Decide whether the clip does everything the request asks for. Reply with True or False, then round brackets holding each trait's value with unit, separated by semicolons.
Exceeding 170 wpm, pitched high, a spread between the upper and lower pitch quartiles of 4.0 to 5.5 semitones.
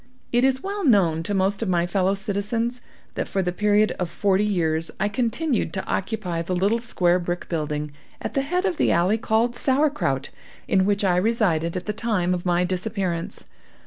True (190 wpm; 195 Hz; 4.5 semitones)